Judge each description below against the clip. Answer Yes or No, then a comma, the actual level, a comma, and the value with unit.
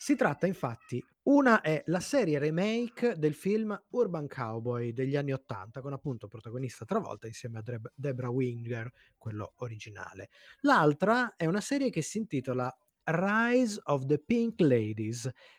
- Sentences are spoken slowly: No, average, 140 wpm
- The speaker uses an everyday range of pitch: No, wide, 8.9 semitones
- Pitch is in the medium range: Yes, medium, 145 Hz